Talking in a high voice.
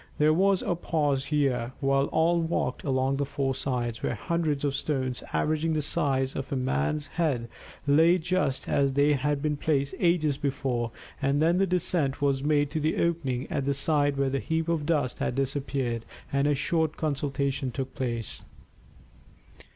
No: medium, 140 Hz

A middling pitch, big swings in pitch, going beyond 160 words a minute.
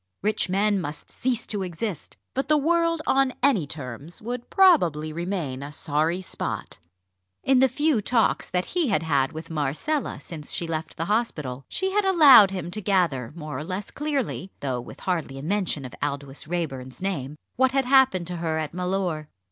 Yes: medium, 180 Hz; wide, 8.4 semitones; average, 180 wpm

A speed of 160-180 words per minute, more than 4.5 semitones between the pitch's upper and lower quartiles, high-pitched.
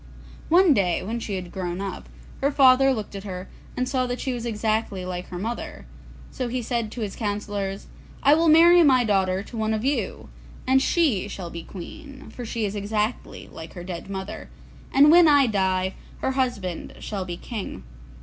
No: average, 190 wpm; wide, 5.4 semitones; high, 220 Hz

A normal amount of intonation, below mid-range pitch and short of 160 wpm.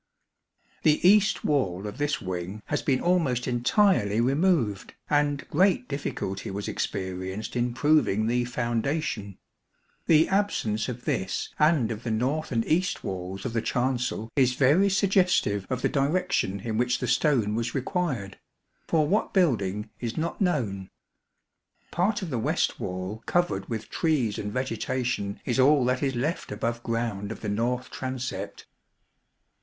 No: wide, 6.2 semitones; low, 125 Hz; average, 150 wpm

